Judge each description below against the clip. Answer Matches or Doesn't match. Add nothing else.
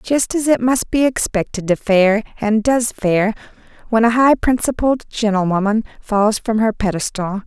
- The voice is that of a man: Doesn't match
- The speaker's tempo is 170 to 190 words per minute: Doesn't match